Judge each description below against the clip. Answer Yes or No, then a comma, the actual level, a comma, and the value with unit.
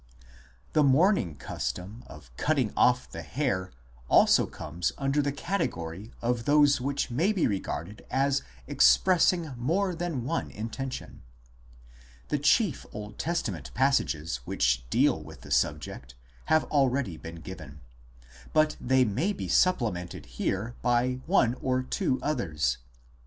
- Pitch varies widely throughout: Yes, wide, 8.1 semitones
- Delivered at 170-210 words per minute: No, slow, 135 wpm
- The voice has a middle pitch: No, low, 125 Hz